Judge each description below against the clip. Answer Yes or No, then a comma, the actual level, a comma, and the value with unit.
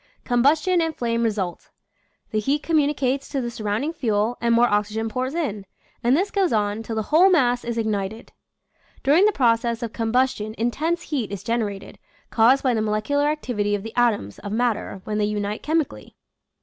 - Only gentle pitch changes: No, average, 4.9 semitones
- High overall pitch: Yes, high, 235 Hz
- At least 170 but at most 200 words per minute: Yes, average, 175 wpm